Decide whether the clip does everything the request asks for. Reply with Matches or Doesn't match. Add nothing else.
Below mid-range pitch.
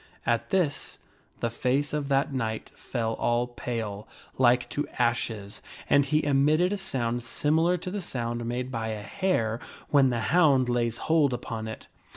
Matches